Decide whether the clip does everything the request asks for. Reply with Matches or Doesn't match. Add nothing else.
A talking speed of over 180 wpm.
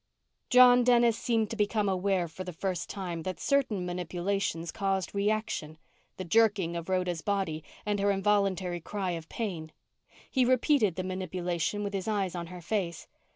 Doesn't match